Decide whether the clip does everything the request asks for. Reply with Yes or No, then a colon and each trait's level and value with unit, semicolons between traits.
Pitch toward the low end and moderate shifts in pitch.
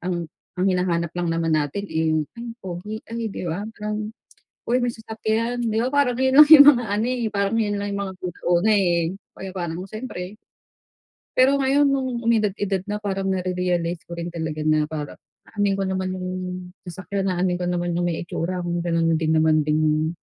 No: medium, 185 Hz; average, 4.1 semitones